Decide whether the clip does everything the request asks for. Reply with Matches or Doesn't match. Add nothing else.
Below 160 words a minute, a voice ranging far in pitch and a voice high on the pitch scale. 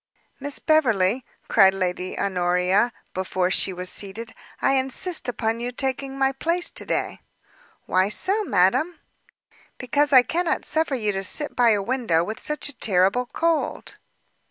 Matches